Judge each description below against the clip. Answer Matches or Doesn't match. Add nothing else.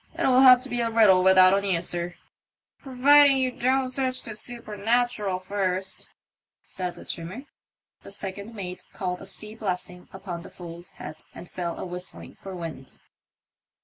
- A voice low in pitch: Doesn't match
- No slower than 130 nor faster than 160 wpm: Matches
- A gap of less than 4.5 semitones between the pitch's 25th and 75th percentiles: Doesn't match